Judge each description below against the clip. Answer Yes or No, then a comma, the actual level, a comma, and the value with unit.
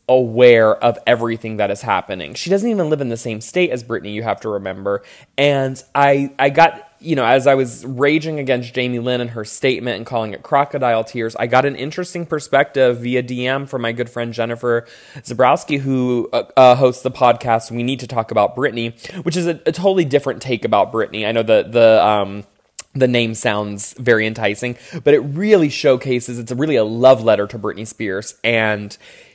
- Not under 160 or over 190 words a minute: No, average, 200 wpm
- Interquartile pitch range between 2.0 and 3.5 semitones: Yes, average, 3.2 semitones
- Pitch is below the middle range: Yes, low, 125 Hz